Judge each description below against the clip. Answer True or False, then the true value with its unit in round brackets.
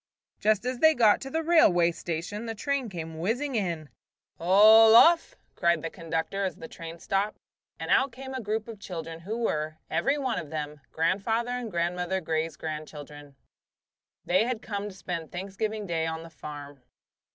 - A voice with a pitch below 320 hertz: True (190 Hz)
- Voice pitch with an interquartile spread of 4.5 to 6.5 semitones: True (5.6 semitones)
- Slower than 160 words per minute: False (175 wpm)